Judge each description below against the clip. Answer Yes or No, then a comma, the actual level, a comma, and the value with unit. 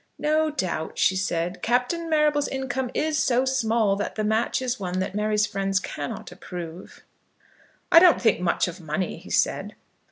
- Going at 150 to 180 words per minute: Yes, average, 165 wpm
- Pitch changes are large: Yes, wide, 6.1 semitones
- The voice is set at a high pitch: Yes, high, 220 Hz